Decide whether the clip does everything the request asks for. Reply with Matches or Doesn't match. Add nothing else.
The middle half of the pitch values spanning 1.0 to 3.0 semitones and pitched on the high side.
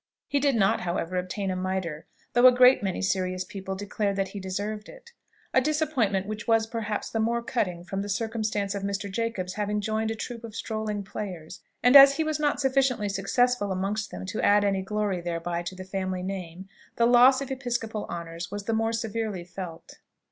Doesn't match